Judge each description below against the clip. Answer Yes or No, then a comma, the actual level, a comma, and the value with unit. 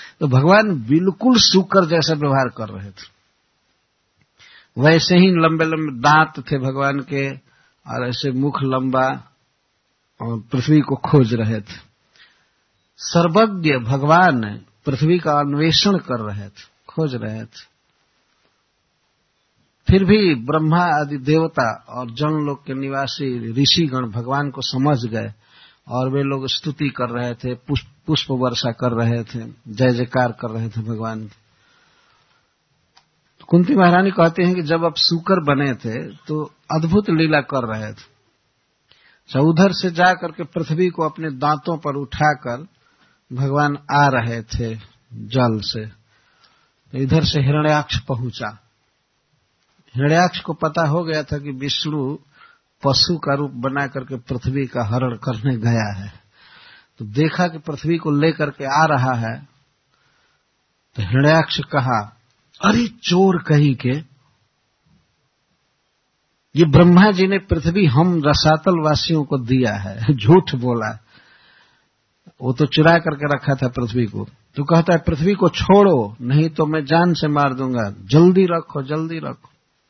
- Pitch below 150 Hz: Yes, medium, 140 Hz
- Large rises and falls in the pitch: No, average, 4.6 semitones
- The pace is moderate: Yes, average, 135 wpm